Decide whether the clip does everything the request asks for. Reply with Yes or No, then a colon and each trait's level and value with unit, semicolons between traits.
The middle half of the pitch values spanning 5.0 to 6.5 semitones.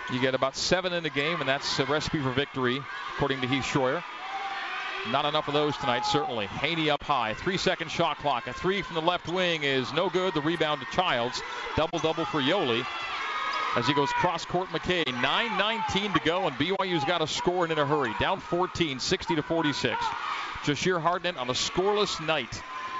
No: average, 4.1 semitones